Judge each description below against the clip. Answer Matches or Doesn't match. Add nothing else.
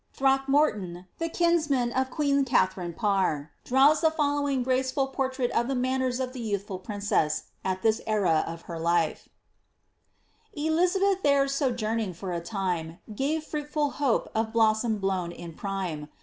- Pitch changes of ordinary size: Doesn't match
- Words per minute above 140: Matches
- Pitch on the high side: Matches